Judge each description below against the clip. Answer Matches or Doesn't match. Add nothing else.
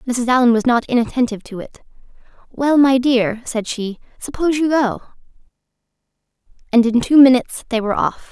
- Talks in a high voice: Matches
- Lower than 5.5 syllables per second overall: Doesn't match